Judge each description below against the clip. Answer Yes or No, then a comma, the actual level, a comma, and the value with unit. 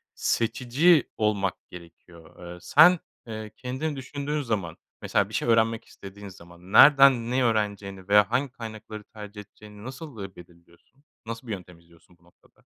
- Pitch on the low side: Yes, low, 110 Hz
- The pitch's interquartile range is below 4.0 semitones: No, average, 5.0 semitones